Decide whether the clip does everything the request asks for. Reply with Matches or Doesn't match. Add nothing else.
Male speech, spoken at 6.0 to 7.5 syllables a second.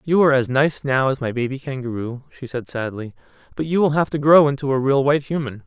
Matches